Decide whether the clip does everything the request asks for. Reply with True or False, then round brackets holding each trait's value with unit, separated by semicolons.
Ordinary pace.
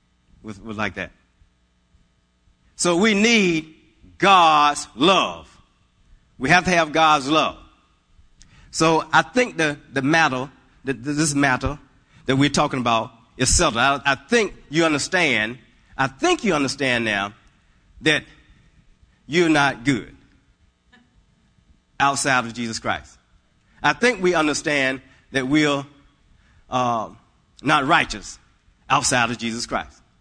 False (120 wpm)